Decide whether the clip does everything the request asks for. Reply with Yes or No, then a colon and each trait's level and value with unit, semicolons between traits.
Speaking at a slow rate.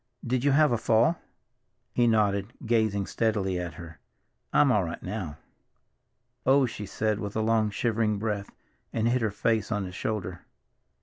No: average, 165 wpm